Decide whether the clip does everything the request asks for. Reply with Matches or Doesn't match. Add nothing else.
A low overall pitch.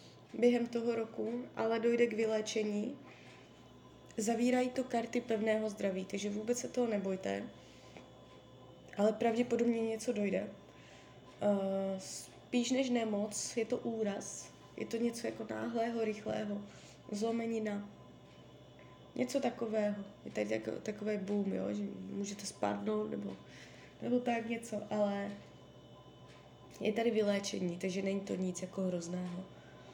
Doesn't match